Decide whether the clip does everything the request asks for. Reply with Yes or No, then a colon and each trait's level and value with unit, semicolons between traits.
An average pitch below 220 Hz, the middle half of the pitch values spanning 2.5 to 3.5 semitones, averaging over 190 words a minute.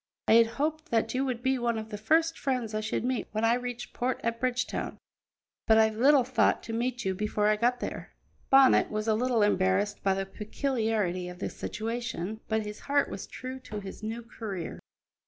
No: high, 225 Hz; average, 2.9 semitones; fast, 205 wpm